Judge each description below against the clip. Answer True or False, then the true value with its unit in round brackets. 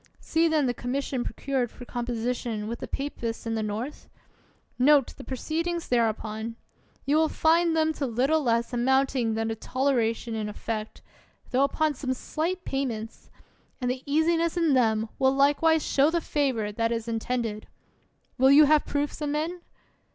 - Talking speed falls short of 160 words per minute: False (165 wpm)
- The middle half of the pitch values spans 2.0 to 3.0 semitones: False (4.7 semitones)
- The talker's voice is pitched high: True (260 Hz)